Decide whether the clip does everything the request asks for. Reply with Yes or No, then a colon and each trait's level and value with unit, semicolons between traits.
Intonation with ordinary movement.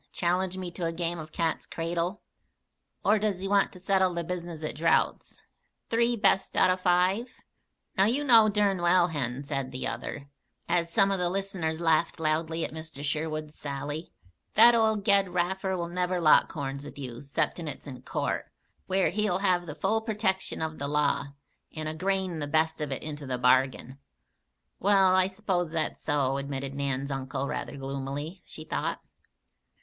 Yes: average, 4.6 semitones